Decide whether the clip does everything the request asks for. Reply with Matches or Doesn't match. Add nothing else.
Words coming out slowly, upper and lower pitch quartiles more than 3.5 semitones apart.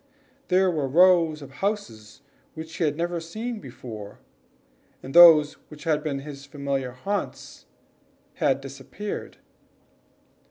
Matches